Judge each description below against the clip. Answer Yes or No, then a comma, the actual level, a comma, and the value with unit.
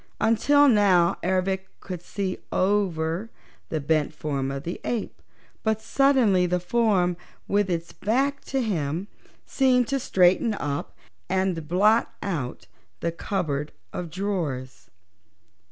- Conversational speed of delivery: No, slow, 120 wpm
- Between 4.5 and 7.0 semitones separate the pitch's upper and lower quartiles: Yes, average, 4.9 semitones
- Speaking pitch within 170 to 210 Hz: Yes, medium, 185 Hz